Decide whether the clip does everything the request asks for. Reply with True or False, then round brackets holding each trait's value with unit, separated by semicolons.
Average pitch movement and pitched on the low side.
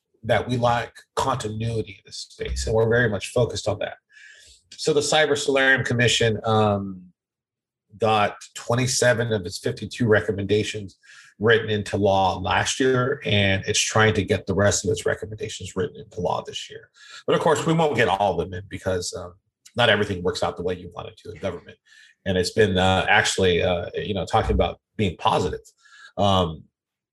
True (4.0 semitones; 110 Hz)